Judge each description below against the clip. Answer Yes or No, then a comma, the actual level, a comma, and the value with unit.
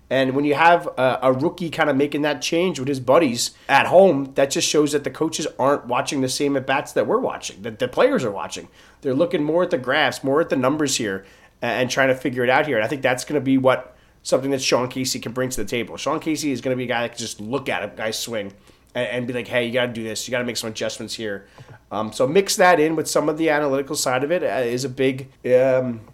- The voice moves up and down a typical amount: Yes, average, 3.3 semitones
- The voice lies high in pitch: No, low, 130 Hz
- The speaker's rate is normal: No, fast, 275 wpm